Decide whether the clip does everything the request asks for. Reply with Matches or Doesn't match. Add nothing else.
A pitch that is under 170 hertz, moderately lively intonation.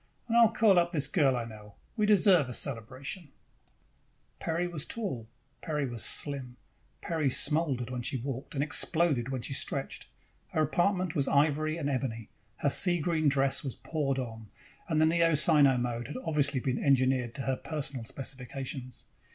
Matches